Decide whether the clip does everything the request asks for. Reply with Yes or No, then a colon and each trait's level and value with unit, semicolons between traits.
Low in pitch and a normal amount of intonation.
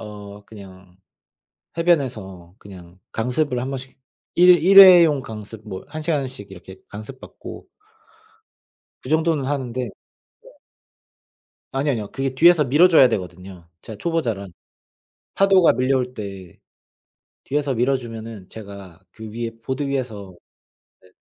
No: low, 120 Hz; wide, 6.1 semitones